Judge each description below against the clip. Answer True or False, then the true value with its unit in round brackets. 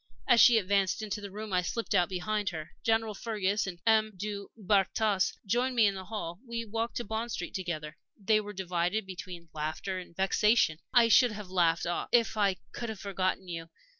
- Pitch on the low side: False (200 Hz)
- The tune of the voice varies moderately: True (3.2 semitones)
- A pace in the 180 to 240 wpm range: True (195 wpm)